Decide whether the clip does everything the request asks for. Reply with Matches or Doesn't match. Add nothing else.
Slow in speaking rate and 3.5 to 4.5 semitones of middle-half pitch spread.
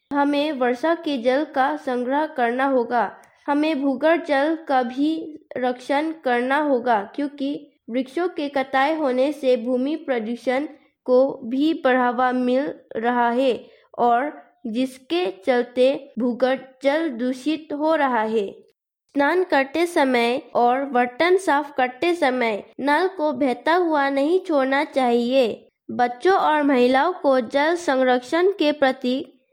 Doesn't match